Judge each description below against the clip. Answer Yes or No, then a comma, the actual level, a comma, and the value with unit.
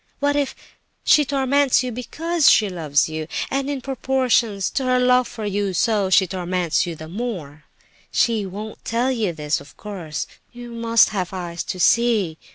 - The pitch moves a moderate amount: No, wide, 5.8 semitones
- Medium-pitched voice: No, high, 220 Hz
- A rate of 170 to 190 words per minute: Yes, average, 175 wpm